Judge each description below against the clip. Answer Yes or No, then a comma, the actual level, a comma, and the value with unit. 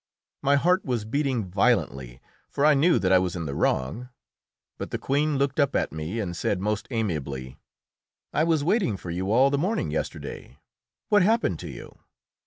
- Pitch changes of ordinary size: No, wide, 8.2 semitones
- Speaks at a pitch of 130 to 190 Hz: No, low, 120 Hz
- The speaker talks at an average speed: Yes, average, 185 wpm